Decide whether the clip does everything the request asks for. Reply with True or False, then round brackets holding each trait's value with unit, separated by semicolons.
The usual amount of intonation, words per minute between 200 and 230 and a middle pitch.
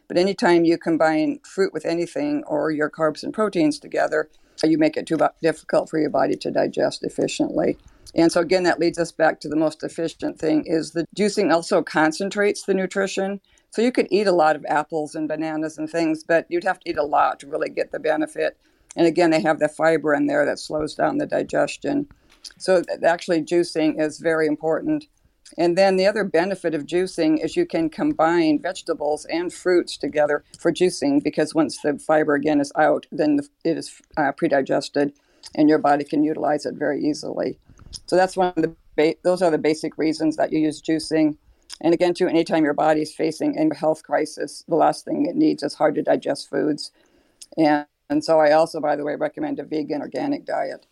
True (3.7 semitones; 205 wpm; 165 Hz)